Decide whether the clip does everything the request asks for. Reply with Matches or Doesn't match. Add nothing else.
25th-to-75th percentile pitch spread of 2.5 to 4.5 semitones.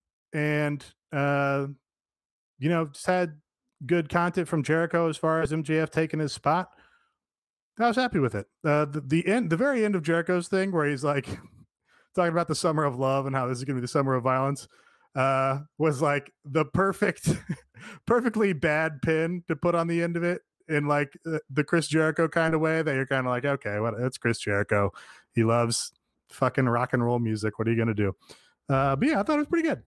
Matches